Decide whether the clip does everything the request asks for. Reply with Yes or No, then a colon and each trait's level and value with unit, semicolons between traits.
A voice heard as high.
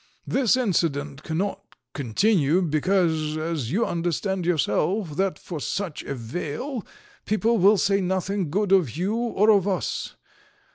No: medium, 180 Hz